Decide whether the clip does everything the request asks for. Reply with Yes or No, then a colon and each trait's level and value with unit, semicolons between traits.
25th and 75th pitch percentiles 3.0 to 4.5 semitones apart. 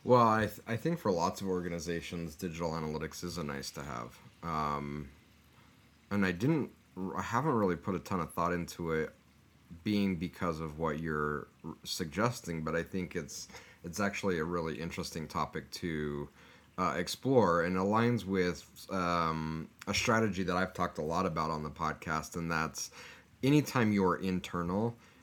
Yes: average, 3.5 semitones